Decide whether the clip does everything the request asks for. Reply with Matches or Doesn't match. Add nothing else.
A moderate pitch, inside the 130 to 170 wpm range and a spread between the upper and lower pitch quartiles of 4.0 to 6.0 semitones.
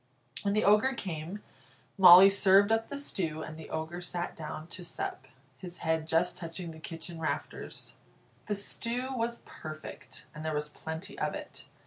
Matches